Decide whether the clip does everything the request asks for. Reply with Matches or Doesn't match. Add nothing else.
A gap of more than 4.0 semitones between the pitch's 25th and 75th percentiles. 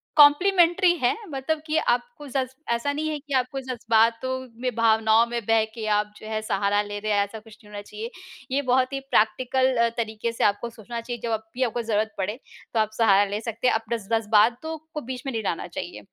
Doesn't match